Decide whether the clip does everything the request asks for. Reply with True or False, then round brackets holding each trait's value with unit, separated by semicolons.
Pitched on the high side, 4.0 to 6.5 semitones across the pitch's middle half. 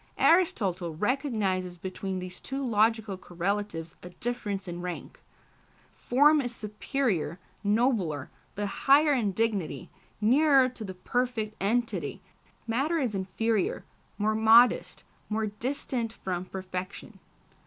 True (215 Hz; 4.7 semitones)